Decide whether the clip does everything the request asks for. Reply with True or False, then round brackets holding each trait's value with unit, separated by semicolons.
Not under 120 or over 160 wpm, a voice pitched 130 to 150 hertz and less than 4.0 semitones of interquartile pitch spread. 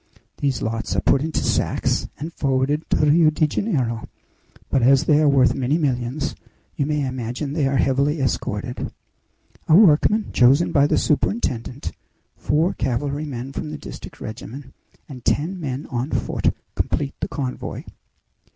True (150 wpm; 140 Hz; 2.9 semitones)